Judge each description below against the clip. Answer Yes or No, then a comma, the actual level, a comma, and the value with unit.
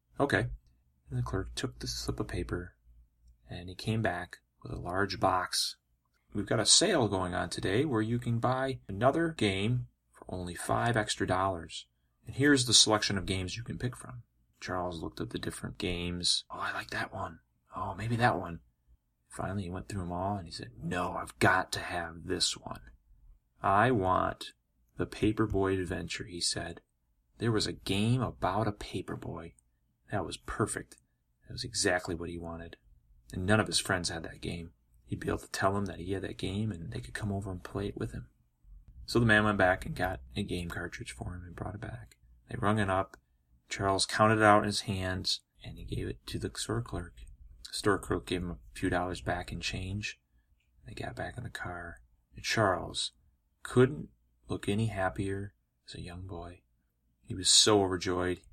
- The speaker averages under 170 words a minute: No, average, 200 wpm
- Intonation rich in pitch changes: Yes, wide, 8.5 semitones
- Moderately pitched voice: No, very low, 90 Hz